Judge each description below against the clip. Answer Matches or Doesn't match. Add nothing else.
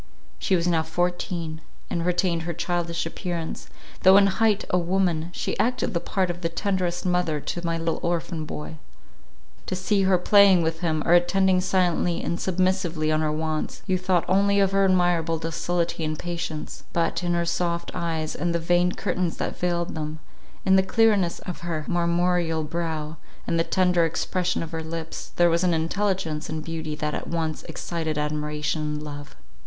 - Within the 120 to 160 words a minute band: Doesn't match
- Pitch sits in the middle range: Matches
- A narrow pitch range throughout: Matches